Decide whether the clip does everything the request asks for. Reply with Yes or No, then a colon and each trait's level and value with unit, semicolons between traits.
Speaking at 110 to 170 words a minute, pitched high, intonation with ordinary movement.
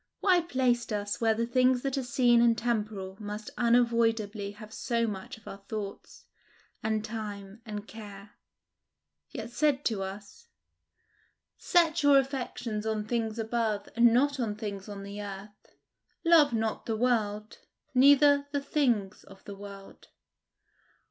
Yes: average, 140 wpm; high, 225 Hz; average, 3.2 semitones